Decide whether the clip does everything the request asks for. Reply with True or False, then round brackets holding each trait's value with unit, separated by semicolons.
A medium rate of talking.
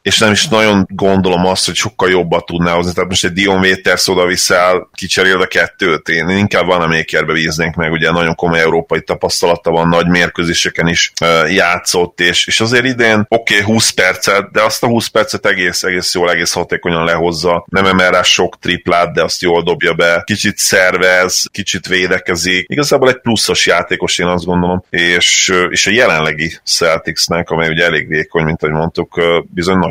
False (185 wpm)